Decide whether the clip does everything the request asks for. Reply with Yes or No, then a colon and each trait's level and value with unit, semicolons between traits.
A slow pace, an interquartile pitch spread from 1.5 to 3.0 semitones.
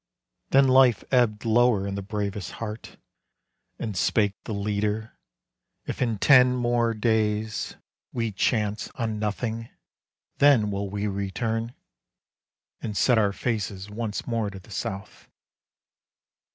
Yes: slow, 125 wpm; narrow, 2.4 semitones